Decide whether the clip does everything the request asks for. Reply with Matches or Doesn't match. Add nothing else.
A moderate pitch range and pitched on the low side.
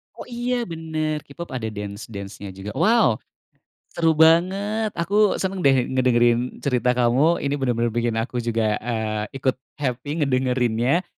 Doesn't match